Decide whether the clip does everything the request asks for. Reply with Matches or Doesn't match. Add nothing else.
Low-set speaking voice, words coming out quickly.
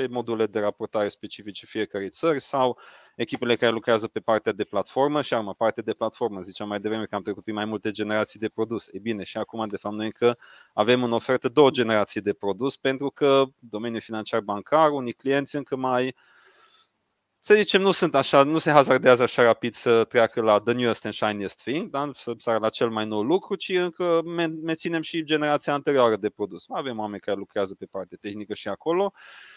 Matches